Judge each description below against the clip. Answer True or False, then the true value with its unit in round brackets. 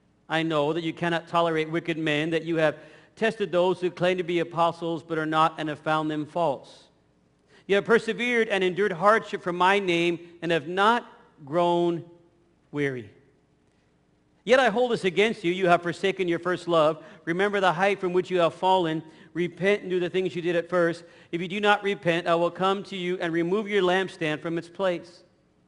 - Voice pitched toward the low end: False (175 Hz)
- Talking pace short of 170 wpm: False (200 wpm)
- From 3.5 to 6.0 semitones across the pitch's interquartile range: False (2.6 semitones)